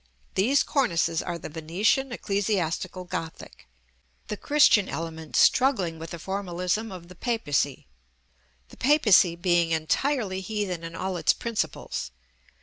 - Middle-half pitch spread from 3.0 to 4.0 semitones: No, average, 4.5 semitones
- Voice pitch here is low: No, medium, 185 Hz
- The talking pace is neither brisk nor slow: No, slow, 125 wpm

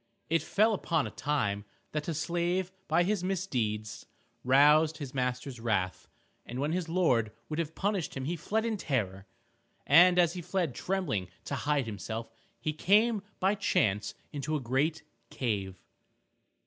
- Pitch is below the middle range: No, medium, 150 Hz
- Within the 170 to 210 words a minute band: No, average, 155 wpm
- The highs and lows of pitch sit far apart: Yes, wide, 6.9 semitones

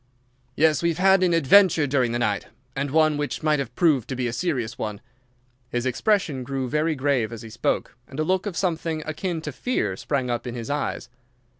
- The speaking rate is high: Yes, fast, 210 wpm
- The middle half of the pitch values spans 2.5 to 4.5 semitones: No, average, 4.9 semitones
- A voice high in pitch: No, medium, 145 Hz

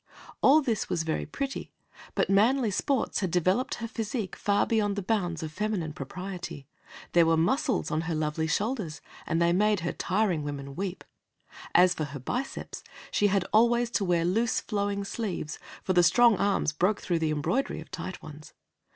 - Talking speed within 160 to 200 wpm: Yes, average, 175 wpm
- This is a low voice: No, high, 190 Hz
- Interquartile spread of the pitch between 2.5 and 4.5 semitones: No, average, 5.0 semitones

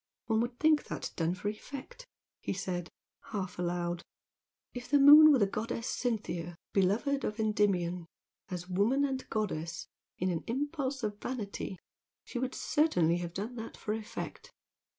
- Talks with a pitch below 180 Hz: No, high, 215 Hz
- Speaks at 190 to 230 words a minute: No, average, 150 wpm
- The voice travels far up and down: Yes, wide, 6.4 semitones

